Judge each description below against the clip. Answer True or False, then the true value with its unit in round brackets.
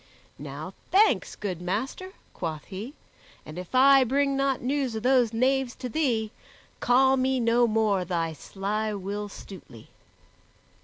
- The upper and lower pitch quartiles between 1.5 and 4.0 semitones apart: False (5.2 semitones)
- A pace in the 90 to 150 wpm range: True (140 wpm)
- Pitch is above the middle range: True (230 Hz)